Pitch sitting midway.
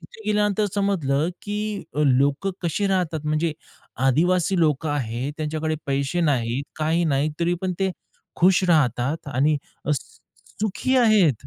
Yes: medium, 160 Hz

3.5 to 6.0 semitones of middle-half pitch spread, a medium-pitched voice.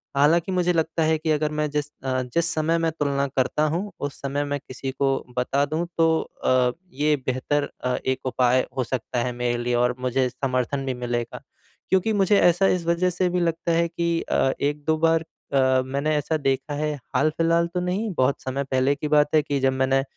Yes: average, 3.9 semitones; medium, 145 Hz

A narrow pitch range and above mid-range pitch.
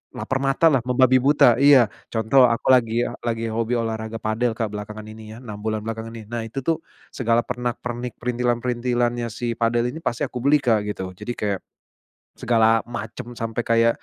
No: narrow, 1.7 semitones; low, 115 Hz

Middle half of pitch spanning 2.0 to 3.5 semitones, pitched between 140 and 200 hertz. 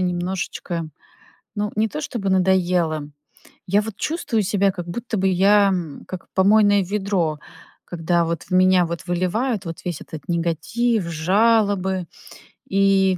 Yes: average, 2.8 semitones; high, 190 Hz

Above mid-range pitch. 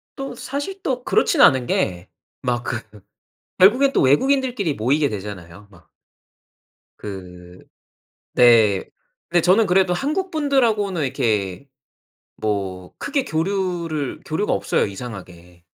No: medium, 140 Hz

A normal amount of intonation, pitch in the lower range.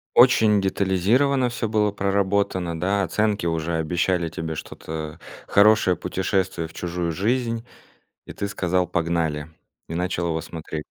Yes: average, 3.7 semitones; very low, 90 Hz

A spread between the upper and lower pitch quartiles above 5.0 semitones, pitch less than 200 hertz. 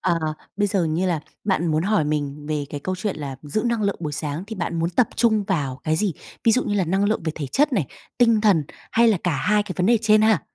Yes: wide, 5.5 semitones; medium, 185 Hz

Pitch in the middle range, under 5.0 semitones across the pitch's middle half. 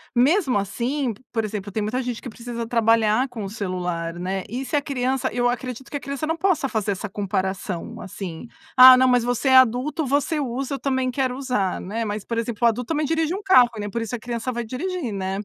No: high, 245 Hz; average, 4.0 semitones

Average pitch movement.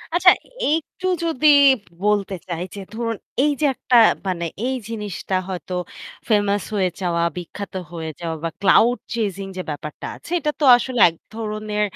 Yes: average, 4.8 semitones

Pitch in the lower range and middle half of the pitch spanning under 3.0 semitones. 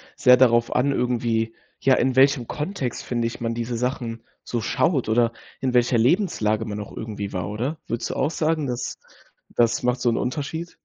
Yes: low, 120 Hz; narrow, 2.6 semitones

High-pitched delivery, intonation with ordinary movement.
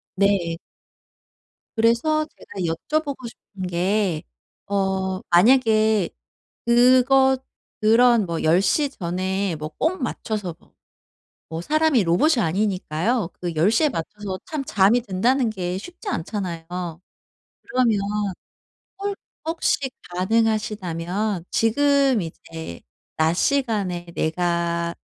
No: high, 205 Hz; wide, 6.0 semitones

